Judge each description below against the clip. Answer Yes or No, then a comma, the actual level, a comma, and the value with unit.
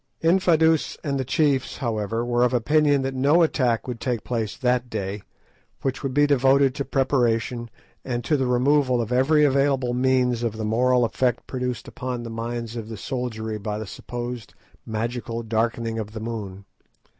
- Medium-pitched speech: No, low, 125 Hz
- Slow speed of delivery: No, average, 170 wpm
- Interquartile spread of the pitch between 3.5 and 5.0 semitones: No, average, 2.7 semitones